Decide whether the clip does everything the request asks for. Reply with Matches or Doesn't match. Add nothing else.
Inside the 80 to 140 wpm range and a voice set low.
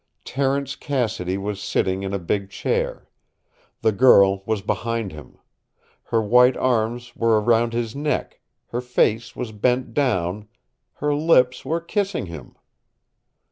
Matches